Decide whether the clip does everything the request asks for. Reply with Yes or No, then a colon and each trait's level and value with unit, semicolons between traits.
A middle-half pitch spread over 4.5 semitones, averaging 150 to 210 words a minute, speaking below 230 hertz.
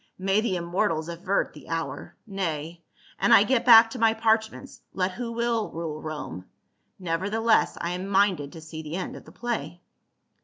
Yes: average, 5.3 semitones; average, 180 wpm; high, 190 Hz